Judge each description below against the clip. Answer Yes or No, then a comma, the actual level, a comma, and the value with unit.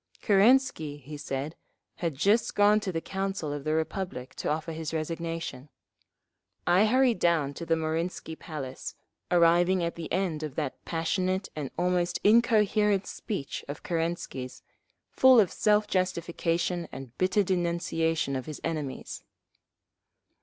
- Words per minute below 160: Yes, slow, 135 wpm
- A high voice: No, medium, 170 Hz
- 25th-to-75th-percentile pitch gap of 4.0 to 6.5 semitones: No, average, 3.6 semitones